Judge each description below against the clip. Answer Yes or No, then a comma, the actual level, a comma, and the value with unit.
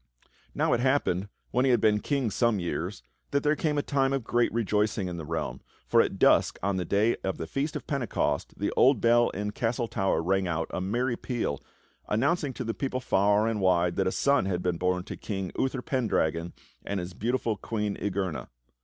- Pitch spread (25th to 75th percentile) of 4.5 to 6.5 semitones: Yes, average, 5.2 semitones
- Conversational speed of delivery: No, fast, 210 wpm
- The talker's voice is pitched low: Yes, low, 105 Hz